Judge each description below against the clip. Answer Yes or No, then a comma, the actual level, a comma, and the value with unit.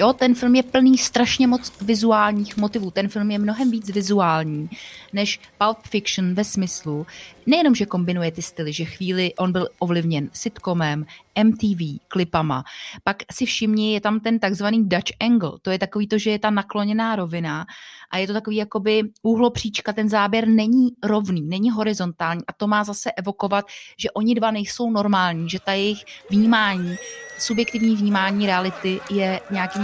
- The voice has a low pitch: No, high, 205 Hz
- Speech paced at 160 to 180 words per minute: Yes, average, 165 wpm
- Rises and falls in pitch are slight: No, average, 3.2 semitones